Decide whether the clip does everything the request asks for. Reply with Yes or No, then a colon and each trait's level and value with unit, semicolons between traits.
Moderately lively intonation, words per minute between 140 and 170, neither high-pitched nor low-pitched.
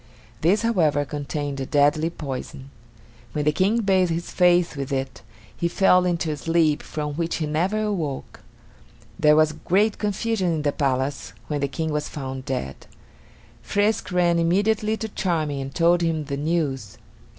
Yes: average, 3.9 semitones; average, 160 wpm; medium, 160 Hz